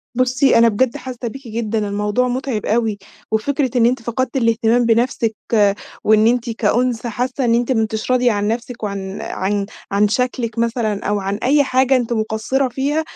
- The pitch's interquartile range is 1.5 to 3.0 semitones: Yes, average, 2.7 semitones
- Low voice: No, high, 235 Hz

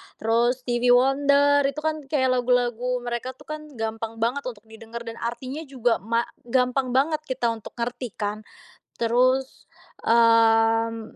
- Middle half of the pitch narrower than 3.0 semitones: Yes, narrow, 2.4 semitones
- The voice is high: Yes, high, 245 Hz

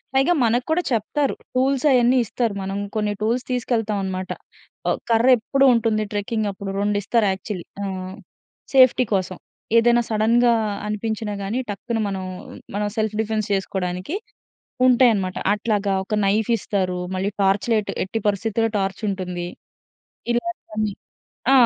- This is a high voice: Yes, high, 215 Hz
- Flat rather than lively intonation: No, average, 3.2 semitones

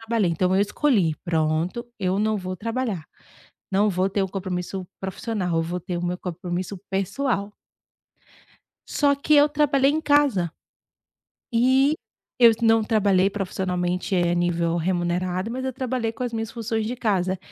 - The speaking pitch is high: Yes, high, 195 Hz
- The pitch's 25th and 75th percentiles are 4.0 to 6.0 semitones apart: Yes, average, 4.6 semitones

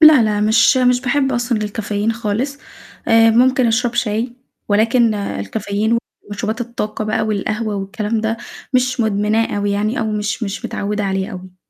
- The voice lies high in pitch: Yes, high, 220 Hz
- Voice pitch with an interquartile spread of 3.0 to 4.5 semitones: No, narrow, 2.4 semitones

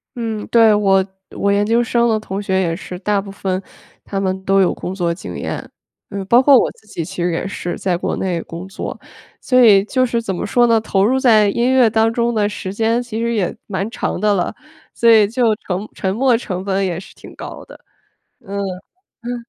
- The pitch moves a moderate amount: Yes, average, 3.4 semitones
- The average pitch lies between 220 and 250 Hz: No, high, 205 Hz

